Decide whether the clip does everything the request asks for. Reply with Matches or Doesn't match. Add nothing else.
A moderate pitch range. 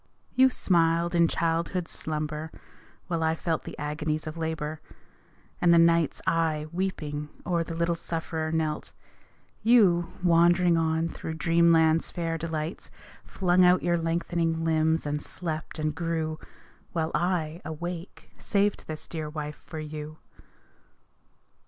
Doesn't match